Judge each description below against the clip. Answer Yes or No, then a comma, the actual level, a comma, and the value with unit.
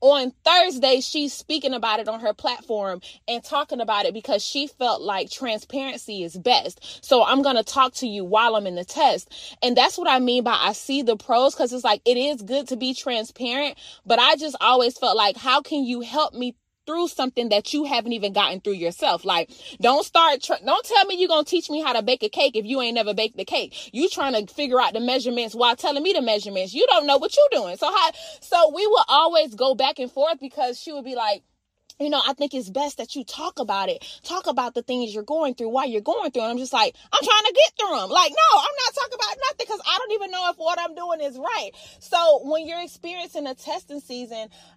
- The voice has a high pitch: Yes, very high, 270 Hz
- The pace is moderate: No, fast, 245 wpm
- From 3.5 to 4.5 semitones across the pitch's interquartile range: No, average, 4.9 semitones